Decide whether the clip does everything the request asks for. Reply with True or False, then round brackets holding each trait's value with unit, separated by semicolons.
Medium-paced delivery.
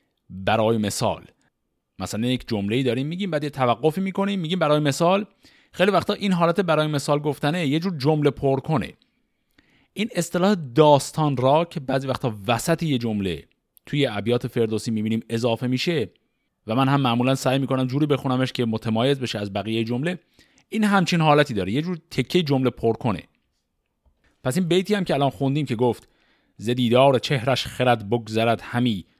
False (165 wpm)